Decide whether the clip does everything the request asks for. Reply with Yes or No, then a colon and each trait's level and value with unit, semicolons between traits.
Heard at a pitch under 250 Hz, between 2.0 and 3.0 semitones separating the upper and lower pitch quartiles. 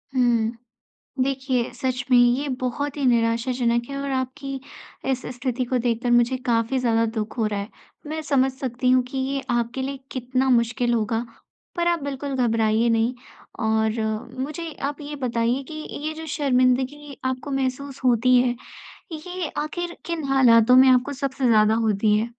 No: very high, 255 Hz; average, 2.7 semitones